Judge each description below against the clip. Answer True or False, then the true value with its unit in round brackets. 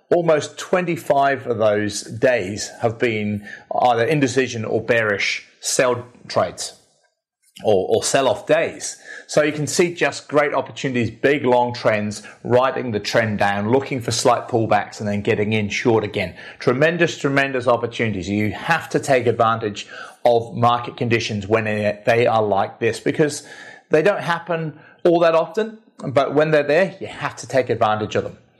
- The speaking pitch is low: True (125 Hz)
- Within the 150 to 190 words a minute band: True (160 wpm)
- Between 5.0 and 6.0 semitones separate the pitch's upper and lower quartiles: True (5.5 semitones)